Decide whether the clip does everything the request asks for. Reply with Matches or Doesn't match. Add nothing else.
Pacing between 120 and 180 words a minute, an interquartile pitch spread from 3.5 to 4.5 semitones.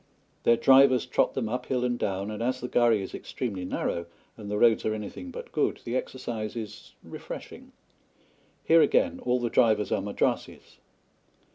Doesn't match